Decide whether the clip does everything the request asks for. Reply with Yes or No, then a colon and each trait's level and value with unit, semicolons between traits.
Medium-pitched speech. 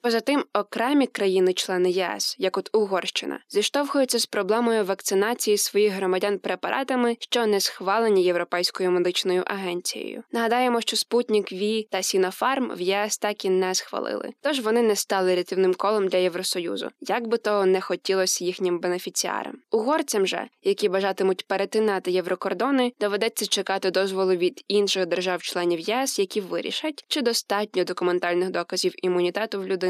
No: high, 195 Hz